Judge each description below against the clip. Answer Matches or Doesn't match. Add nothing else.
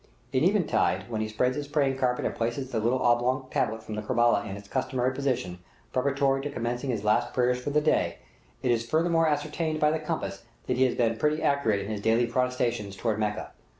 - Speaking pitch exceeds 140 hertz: Doesn't match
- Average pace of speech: Doesn't match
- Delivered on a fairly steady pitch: Doesn't match